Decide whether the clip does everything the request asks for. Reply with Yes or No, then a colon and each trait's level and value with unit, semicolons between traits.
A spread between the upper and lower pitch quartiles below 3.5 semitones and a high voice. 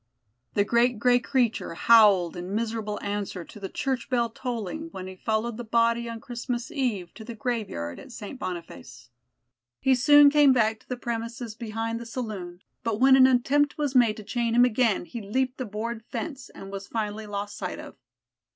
Yes: average, 3.1 semitones; high, 230 Hz